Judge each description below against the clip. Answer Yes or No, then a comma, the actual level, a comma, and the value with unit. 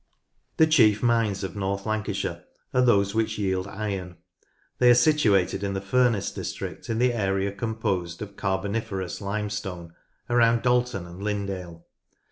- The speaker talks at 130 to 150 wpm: Yes, average, 140 wpm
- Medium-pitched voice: No, low, 100 Hz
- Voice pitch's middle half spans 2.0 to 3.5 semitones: Yes, average, 3.1 semitones